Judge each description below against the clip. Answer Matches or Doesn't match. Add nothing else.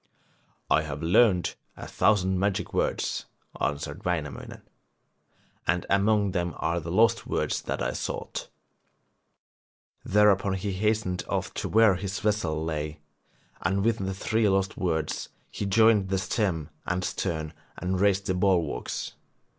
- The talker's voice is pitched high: Doesn't match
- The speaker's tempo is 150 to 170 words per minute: Doesn't match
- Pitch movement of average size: Matches